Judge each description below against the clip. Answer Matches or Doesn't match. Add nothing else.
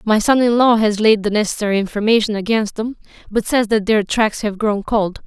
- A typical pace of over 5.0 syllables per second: Matches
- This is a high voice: Matches